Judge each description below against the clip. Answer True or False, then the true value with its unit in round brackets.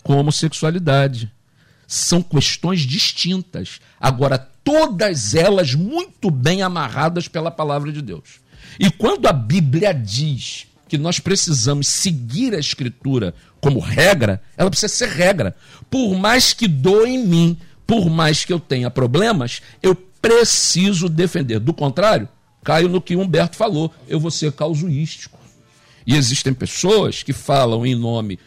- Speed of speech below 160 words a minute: True (135 wpm)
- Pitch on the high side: False (155 Hz)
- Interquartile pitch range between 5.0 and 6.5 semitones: True (5.4 semitones)